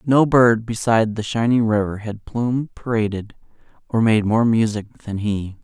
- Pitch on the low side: Yes, low, 110 Hz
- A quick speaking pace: No, average, 160 wpm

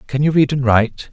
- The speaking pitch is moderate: No, low, 130 Hz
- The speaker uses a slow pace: No, fast, 270 wpm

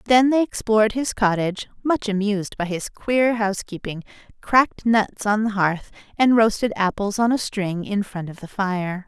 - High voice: Yes, high, 210 Hz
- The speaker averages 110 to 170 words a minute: No, average, 180 wpm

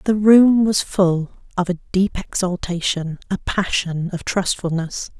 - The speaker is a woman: Yes, female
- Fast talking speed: No, average, 140 wpm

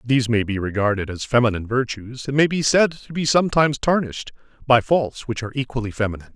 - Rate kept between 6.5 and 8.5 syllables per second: Yes, 6.7 syllables/s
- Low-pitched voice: Yes, low, 125 Hz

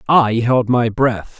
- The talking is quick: No, average, 170 wpm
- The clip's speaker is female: No, male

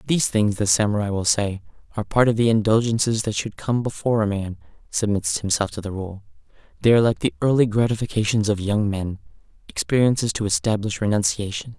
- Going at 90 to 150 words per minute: No, average, 180 wpm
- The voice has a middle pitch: No, low, 110 Hz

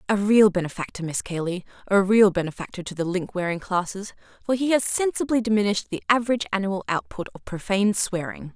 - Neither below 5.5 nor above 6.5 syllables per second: Yes, 6.2 syllables/s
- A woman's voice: Yes, female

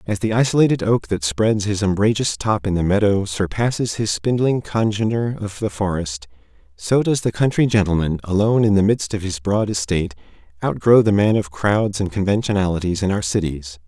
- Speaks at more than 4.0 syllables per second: Yes, 5.4 syllables/s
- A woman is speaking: No, male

